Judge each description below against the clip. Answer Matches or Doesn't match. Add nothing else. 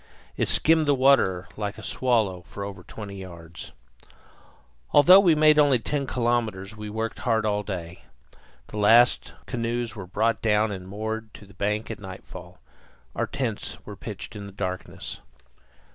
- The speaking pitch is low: Matches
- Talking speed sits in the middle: Matches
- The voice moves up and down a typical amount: Matches